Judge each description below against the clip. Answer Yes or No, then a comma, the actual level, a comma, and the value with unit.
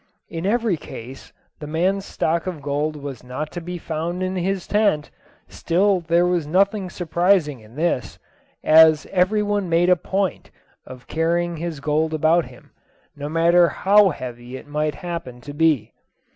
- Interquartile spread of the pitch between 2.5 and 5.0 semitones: Yes, average, 3.4 semitones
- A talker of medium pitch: Yes, medium, 165 Hz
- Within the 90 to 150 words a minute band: No, average, 160 wpm